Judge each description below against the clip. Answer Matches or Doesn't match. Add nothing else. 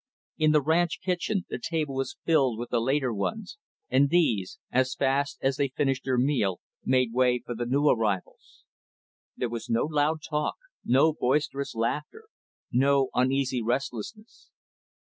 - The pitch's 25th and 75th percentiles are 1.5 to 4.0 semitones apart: Matches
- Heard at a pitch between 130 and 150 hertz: Matches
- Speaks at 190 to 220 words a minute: Doesn't match